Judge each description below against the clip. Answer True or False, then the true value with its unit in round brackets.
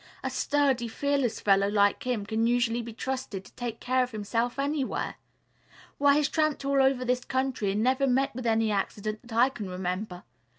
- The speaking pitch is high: True (245 Hz)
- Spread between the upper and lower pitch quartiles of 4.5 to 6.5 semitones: False (3.8 semitones)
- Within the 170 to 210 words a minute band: True (185 wpm)